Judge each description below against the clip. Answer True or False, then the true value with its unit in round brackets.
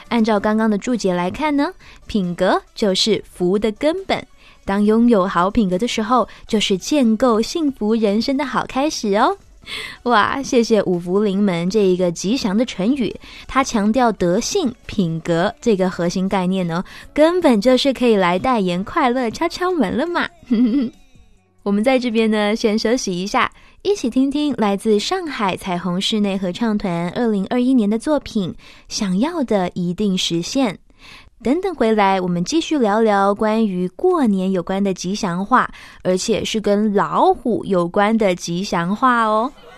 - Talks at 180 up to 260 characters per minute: True (240 characters per minute)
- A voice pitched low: False (215 Hz)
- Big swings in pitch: False (4.9 semitones)